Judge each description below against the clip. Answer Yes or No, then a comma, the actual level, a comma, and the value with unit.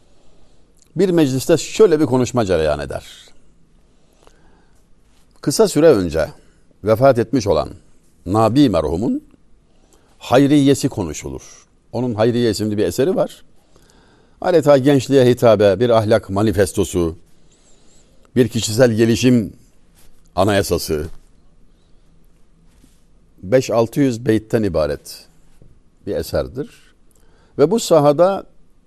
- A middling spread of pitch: No, wide, 7.4 semitones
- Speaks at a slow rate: Yes, slow, 85 wpm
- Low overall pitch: Yes, low, 115 Hz